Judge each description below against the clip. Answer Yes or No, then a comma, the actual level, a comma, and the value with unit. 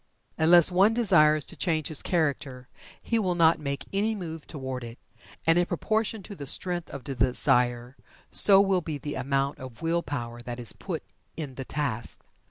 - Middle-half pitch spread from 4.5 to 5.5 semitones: Yes, average, 5.1 semitones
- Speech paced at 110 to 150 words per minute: No, average, 180 wpm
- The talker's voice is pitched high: No, medium, 155 Hz